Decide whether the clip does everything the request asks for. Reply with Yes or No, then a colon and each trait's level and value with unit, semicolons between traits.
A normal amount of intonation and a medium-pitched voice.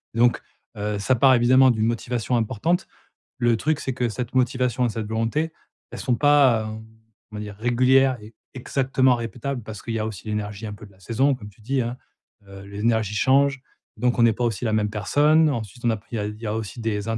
No: average, 3.2 semitones; low, 115 Hz